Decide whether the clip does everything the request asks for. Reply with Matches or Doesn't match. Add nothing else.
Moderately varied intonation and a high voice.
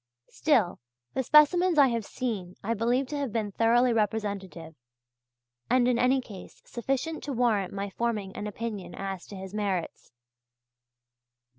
Matches